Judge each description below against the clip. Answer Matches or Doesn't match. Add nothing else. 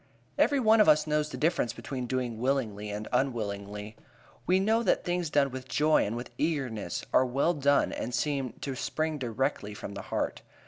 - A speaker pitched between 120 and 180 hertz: Matches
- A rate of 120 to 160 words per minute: Doesn't match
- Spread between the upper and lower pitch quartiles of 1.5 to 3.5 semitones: Doesn't match